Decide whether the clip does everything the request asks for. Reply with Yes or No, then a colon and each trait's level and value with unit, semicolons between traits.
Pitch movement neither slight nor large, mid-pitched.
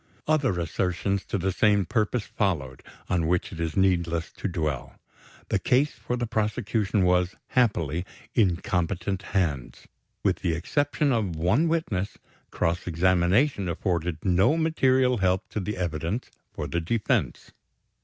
No: average, 4.5 semitones; very low, 95 Hz